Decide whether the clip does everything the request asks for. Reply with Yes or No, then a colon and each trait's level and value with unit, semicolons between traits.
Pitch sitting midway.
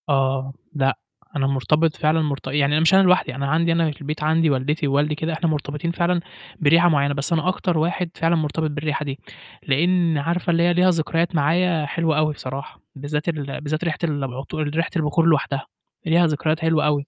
Yes: medium, 155 Hz